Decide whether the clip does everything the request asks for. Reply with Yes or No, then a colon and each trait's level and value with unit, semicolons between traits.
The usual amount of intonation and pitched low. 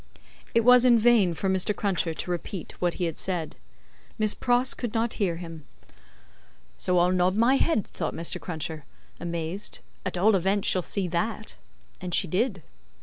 No: average, 4.1 semitones; medium, 185 Hz